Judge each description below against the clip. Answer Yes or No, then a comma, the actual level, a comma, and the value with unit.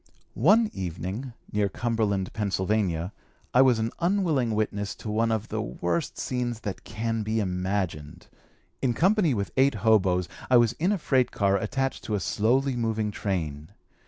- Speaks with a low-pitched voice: Yes, low, 110 Hz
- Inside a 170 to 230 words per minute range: No, average, 160 wpm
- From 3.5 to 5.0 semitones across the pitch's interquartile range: Yes, average, 4.5 semitones